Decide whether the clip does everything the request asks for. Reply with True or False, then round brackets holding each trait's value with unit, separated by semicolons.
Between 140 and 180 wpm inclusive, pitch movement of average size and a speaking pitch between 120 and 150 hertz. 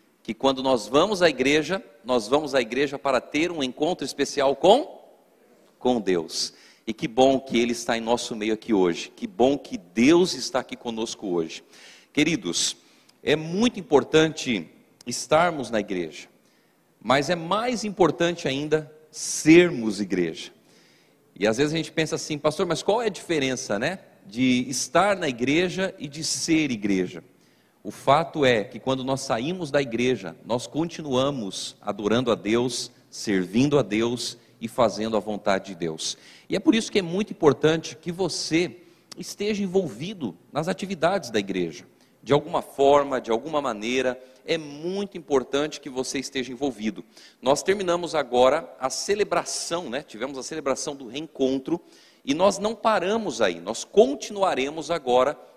False (155 wpm; 5.8 semitones; 140 Hz)